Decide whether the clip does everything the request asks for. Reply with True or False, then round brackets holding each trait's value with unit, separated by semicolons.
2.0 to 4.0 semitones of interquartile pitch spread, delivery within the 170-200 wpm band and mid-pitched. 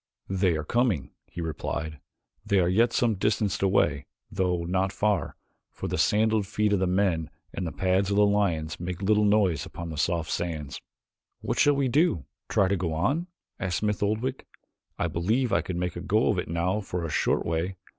False (3.7 semitones; 195 wpm; 95 Hz)